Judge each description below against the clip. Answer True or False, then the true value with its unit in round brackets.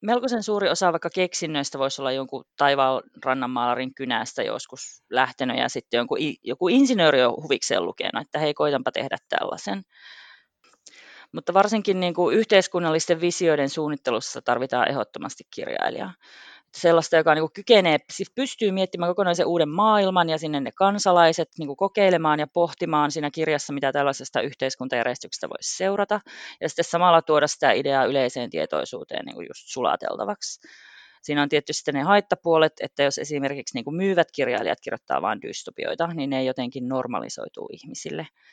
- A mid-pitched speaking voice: True (160 Hz)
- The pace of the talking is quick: False (140 wpm)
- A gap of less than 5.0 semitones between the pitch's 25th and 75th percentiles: False (5.3 semitones)